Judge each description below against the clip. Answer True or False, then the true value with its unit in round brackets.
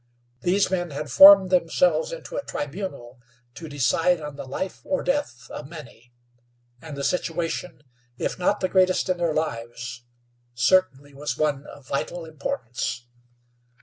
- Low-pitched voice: False (155 Hz)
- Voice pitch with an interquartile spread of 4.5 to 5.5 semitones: True (5.1 semitones)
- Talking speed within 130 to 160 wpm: True (145 wpm)